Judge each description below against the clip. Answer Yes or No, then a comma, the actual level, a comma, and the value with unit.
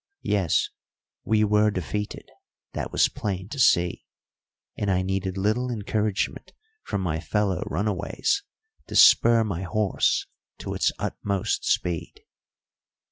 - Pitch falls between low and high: No, low, 100 Hz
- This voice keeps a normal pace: No, slow, 120 wpm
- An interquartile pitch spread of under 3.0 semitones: Yes, narrow, 2.4 semitones